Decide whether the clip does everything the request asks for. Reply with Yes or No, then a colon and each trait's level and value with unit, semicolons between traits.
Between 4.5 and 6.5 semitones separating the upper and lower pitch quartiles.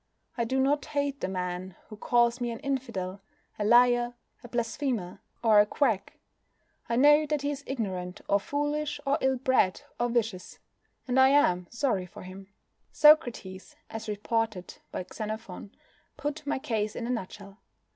Yes: average, 5.2 semitones